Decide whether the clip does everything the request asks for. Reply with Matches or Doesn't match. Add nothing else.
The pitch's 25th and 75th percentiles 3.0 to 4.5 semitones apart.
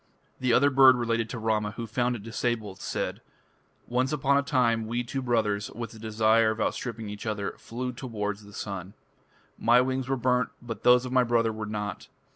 Doesn't match